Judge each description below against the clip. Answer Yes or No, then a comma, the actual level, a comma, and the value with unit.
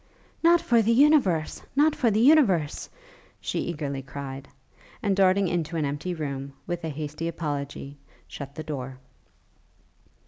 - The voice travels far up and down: Yes, wide, 6.1 semitones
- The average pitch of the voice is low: No, medium, 160 Hz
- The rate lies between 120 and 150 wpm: Yes, average, 140 wpm